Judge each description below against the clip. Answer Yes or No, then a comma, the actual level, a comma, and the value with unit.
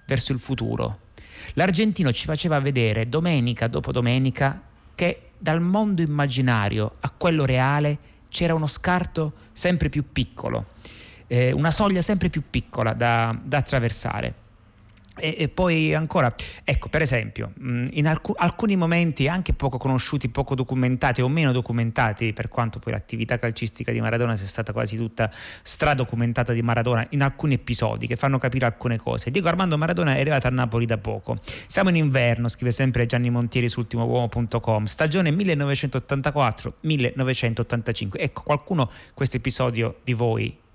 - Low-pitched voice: Yes, low, 125 Hz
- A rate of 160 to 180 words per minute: No, average, 145 wpm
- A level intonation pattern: No, average, 4.3 semitones